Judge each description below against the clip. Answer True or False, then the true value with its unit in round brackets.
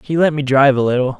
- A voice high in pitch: False (135 Hz)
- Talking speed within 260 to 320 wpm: True (300 wpm)